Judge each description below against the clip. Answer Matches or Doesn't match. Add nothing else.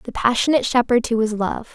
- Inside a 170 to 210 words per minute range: Matches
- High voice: Matches